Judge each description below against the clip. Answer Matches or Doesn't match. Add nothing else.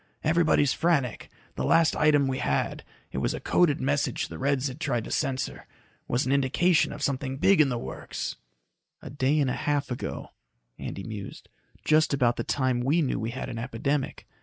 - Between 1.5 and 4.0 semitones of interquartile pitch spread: Matches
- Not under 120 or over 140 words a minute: Doesn't match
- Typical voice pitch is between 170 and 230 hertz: Doesn't match